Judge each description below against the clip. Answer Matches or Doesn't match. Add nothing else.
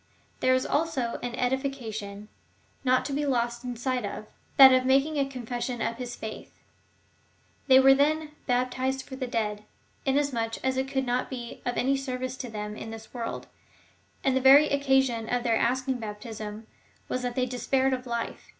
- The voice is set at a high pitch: Matches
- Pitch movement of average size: Doesn't match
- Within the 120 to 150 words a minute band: Doesn't match